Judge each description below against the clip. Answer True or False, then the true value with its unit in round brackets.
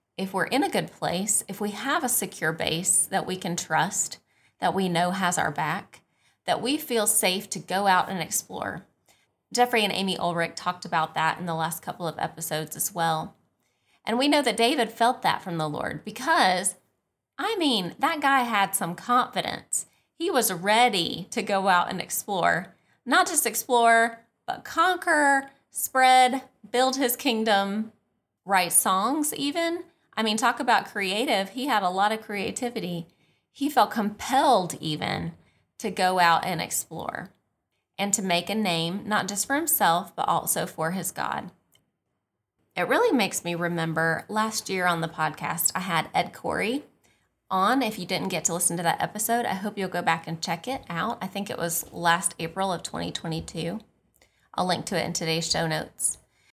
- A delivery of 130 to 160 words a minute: False (175 wpm)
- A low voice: False (195 Hz)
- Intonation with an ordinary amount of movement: False (5.7 semitones)